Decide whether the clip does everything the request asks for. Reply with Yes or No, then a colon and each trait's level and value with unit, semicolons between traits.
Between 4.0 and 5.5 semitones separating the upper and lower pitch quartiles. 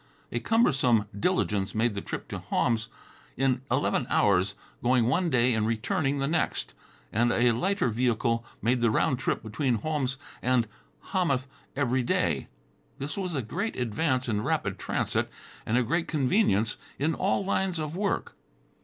Yes: average, 5.2 semitones